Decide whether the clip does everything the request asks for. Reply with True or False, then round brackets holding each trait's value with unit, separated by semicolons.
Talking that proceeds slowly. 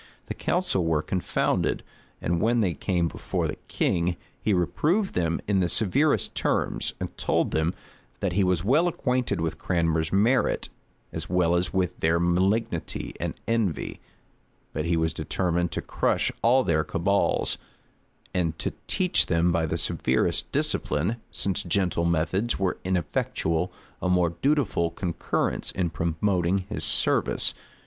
False (145 wpm)